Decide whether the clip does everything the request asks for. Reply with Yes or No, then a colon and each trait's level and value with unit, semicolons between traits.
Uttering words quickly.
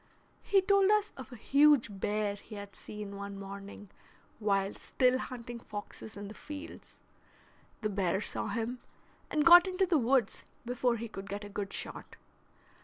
No: average, 165 wpm